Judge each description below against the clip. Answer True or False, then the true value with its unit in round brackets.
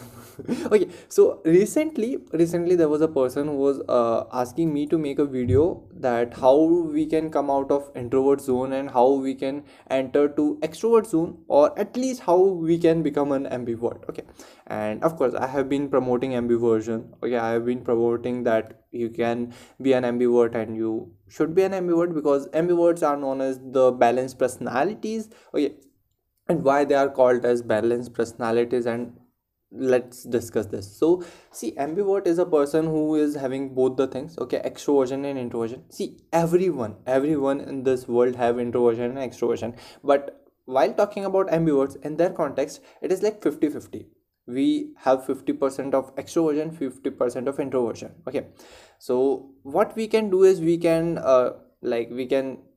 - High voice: False (135 Hz)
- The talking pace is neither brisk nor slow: True (175 wpm)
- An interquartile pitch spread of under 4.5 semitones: False (4.8 semitones)